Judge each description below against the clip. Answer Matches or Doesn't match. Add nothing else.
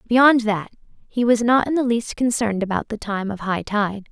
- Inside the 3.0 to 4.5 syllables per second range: Doesn't match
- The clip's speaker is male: Doesn't match